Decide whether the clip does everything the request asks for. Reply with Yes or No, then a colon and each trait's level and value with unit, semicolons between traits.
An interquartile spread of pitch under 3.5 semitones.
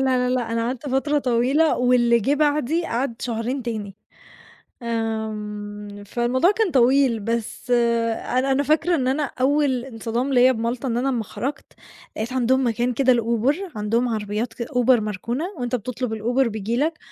Yes: average, 2.7 semitones